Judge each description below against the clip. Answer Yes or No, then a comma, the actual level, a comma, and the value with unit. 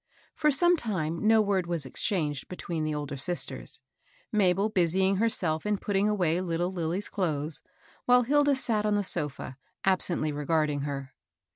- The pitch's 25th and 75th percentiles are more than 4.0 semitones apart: Yes, average, 5.2 semitones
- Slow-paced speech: No, average, 155 wpm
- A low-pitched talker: No, medium, 180 Hz